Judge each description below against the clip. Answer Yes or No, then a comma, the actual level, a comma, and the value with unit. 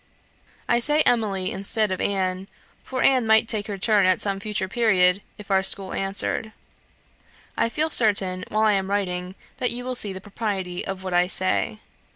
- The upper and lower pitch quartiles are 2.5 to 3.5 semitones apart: Yes, average, 2.8 semitones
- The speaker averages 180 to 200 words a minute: Yes, average, 185 wpm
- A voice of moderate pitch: No, high, 200 Hz